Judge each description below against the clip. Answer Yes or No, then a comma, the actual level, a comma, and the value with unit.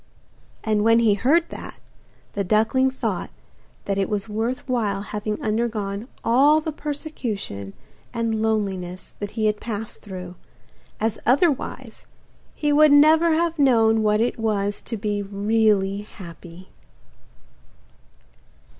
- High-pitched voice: Yes, high, 220 Hz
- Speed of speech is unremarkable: No, slow, 125 wpm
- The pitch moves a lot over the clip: No, average, 3.8 semitones